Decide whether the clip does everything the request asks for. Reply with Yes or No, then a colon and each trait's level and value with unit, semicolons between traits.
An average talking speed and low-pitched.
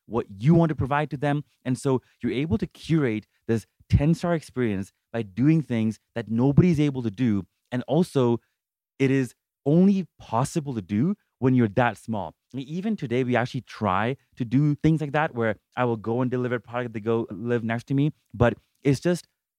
Yes: average, 190 wpm; low, 125 Hz